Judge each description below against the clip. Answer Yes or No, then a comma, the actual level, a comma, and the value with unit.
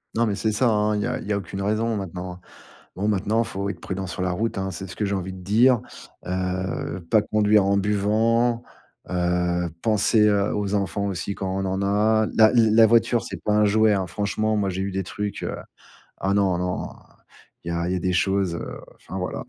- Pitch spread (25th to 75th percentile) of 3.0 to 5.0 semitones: No, narrow, 2.5 semitones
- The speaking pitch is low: Yes, low, 100 Hz